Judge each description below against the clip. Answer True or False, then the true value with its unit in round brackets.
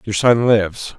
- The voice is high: False (110 Hz)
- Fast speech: False (180 wpm)